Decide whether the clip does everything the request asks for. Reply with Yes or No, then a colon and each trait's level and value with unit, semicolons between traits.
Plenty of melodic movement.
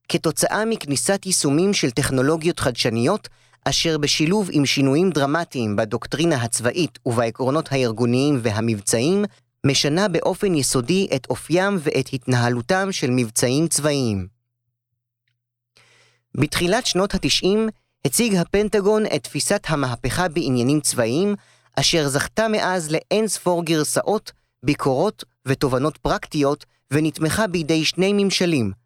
Yes: wide, 6.1 semitones